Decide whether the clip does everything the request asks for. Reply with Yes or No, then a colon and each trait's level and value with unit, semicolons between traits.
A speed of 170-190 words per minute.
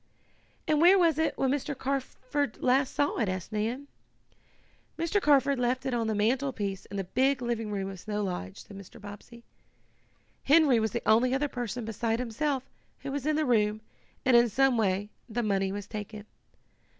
Yes: average, 180 wpm